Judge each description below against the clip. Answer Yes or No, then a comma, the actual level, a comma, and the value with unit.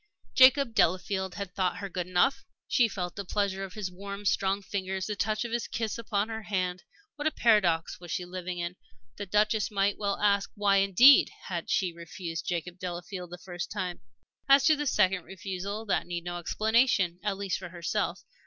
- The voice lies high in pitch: Yes, high, 195 Hz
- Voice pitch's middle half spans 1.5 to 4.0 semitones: Yes, average, 2.8 semitones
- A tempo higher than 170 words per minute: Yes, average, 195 wpm